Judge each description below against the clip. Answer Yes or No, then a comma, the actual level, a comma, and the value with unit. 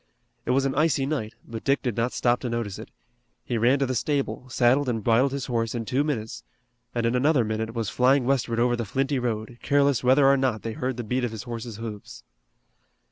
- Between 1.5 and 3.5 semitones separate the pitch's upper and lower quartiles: Yes, average, 2.9 semitones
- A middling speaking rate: No, fast, 225 wpm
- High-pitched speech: No, low, 125 Hz